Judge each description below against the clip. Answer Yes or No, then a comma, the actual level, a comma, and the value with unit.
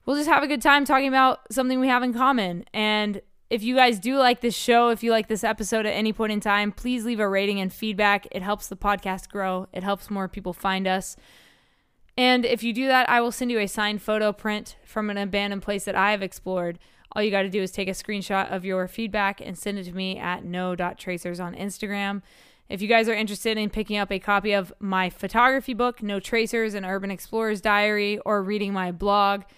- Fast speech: Yes, fast, 230 wpm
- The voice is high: Yes, high, 205 Hz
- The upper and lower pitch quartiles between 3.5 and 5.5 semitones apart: No, average, 2.7 semitones